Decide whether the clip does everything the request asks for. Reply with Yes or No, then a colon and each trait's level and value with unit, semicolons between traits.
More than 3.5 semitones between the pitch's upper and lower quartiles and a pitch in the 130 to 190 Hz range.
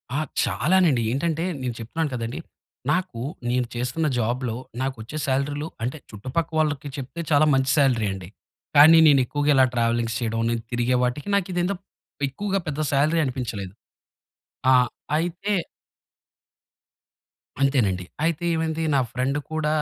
Yes: average, 4.7 semitones; low, 135 Hz